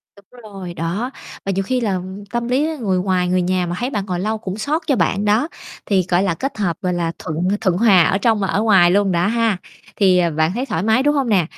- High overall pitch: Yes, high, 195 Hz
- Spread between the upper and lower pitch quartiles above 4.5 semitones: No, average, 4.0 semitones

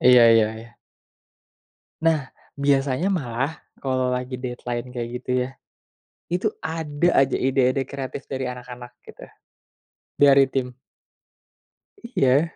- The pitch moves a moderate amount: No, narrow, 2.2 semitones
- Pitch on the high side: No, low, 130 Hz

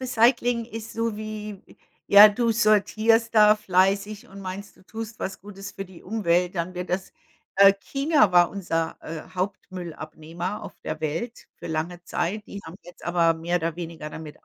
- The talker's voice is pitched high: Yes, high, 195 Hz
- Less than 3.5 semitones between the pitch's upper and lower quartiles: No, average, 3.8 semitones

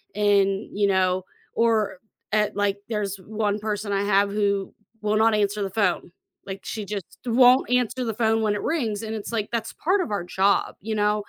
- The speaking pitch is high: Yes, high, 210 Hz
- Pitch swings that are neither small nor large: No, narrow, 1.8 semitones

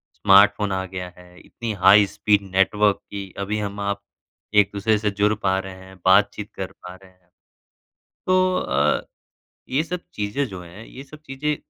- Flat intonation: Yes, narrow, 2.1 semitones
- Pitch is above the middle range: No, low, 100 Hz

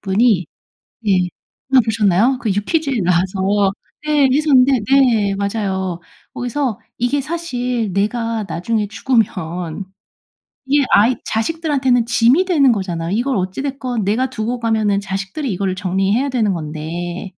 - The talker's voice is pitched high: Yes, high, 220 Hz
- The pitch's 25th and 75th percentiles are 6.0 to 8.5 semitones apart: No, average, 5.2 semitones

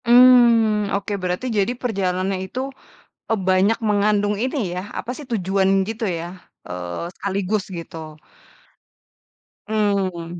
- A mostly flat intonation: No, average, 3.3 semitones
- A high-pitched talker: Yes, high, 200 Hz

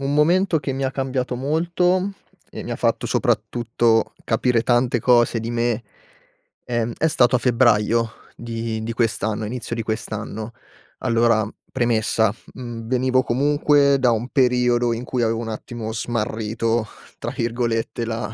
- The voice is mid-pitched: No, low, 120 Hz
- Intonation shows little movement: Yes, narrow, 2.3 semitones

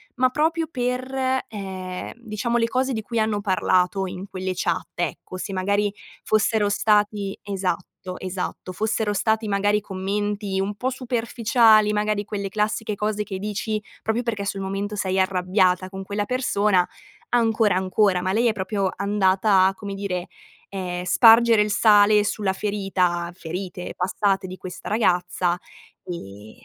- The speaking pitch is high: Yes, high, 205 Hz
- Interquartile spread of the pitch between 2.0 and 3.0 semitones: Yes, narrow, 2.6 semitones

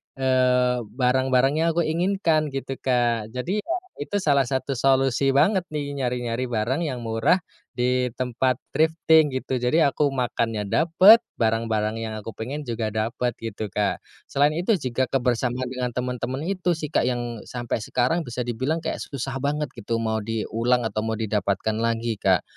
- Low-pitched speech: Yes, low, 125 Hz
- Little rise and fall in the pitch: No, average, 3.7 semitones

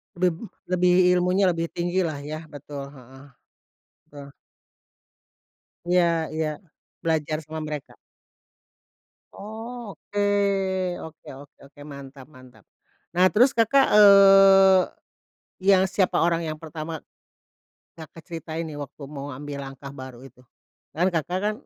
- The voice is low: No, medium, 165 Hz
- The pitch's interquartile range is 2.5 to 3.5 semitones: No, average, 4.6 semitones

